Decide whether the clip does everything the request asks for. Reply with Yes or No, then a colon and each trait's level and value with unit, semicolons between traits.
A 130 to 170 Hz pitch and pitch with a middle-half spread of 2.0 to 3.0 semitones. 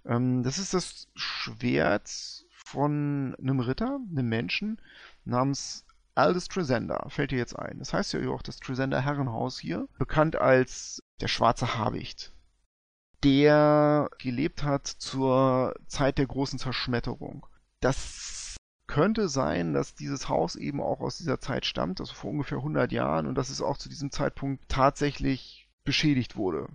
Yes: low, 135 Hz; narrow, 2.5 semitones